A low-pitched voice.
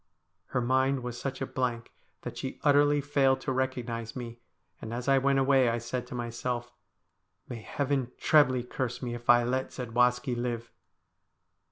Yes: low, 125 Hz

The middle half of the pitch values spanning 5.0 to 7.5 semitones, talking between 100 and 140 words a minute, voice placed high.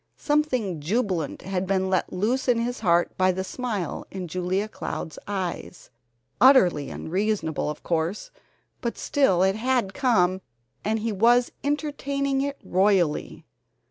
Yes: wide, 5.4 semitones; slow, 135 wpm; high, 200 Hz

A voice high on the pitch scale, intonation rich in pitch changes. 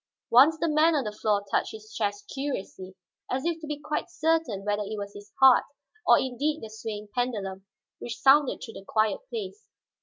Yes: high, 235 Hz; wide, 6.4 semitones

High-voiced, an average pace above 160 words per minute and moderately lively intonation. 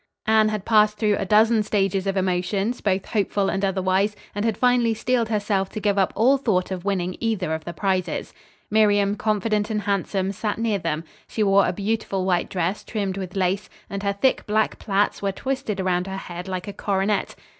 No: high, 200 Hz; average, 200 wpm; narrow, 2.1 semitones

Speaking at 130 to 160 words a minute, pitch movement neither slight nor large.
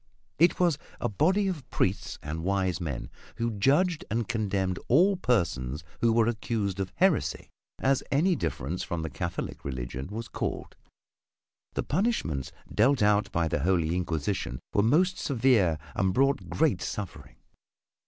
No: average, 145 wpm; wide, 8.2 semitones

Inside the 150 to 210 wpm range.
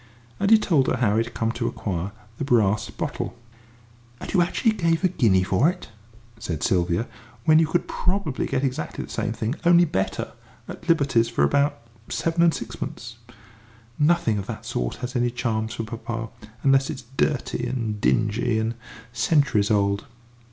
Yes: average, 170 wpm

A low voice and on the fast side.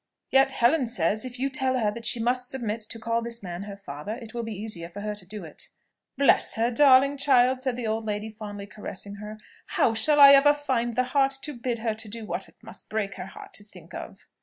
No: high, 230 Hz; fast, 235 wpm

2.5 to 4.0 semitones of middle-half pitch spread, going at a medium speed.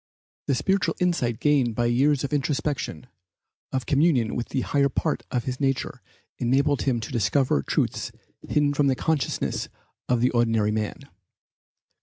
Yes: average, 3.2 semitones; average, 150 wpm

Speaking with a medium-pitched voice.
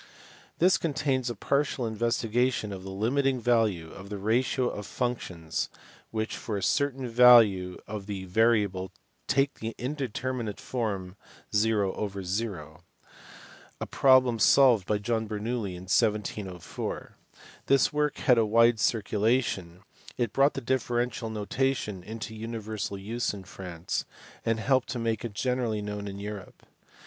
No: low, 110 Hz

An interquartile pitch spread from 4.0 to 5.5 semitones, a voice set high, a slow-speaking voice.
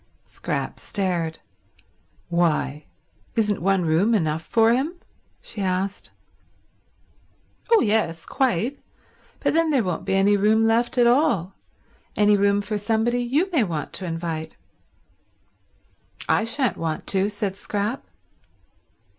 Yes: average, 4.8 semitones; high, 205 Hz; slow, 120 wpm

